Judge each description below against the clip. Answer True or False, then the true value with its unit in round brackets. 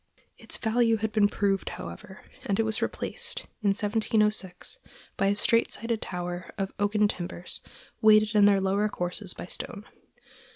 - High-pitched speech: True (205 Hz)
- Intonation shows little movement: True (2.1 semitones)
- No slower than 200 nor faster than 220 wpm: False (155 wpm)